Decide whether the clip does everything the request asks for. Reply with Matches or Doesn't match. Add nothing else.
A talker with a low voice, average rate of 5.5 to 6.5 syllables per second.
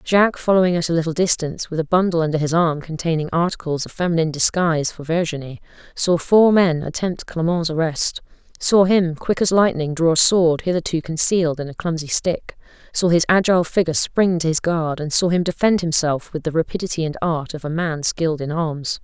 Doesn't match